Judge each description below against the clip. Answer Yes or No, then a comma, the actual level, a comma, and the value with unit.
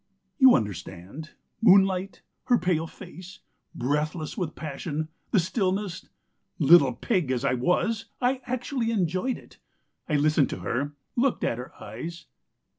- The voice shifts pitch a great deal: Yes, wide, 5.7 semitones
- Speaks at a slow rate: Yes, slow, 130 wpm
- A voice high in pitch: No, medium, 175 Hz